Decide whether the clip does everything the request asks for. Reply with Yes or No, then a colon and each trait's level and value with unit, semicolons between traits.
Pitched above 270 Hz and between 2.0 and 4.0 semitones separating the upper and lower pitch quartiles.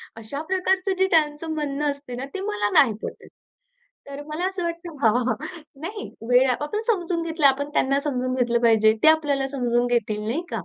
No: very high, 280 Hz; average, 5.1 semitones